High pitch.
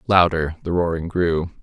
No: very low, 85 Hz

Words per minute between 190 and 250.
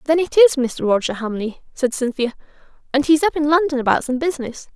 Yes: average, 200 wpm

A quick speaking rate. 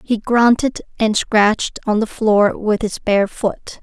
No: average, 175 wpm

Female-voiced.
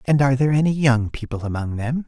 No: male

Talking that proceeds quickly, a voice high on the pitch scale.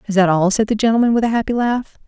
Yes: fast, 290 wpm; high, 215 Hz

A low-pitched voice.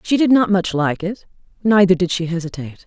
No: medium, 185 Hz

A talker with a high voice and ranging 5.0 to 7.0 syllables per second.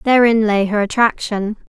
No: high, 215 Hz; 4.7 syllables/s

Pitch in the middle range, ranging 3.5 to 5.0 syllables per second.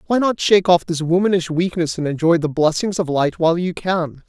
No: medium, 170 Hz; 5.6 syllables/s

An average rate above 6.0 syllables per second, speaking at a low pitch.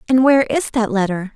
No: 6.9 syllables/s; high, 235 Hz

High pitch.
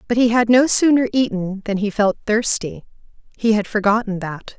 Yes: high, 215 Hz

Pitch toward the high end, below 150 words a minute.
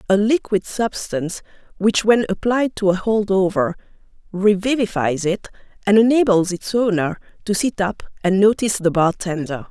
Yes: high, 200 Hz; average, 140 wpm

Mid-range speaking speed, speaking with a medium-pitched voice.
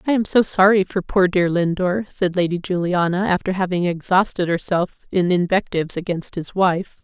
Yes: average, 170 wpm; medium, 180 Hz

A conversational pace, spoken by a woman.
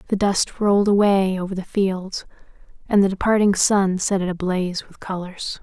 Yes: average, 170 wpm; female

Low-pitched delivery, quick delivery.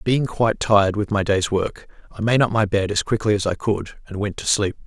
Yes: low, 105 Hz; fast, 260 wpm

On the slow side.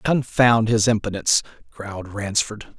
Yes: slow, 110 wpm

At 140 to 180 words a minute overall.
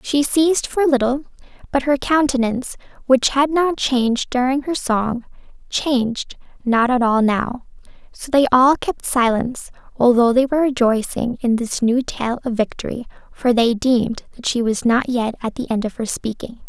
Yes: average, 175 wpm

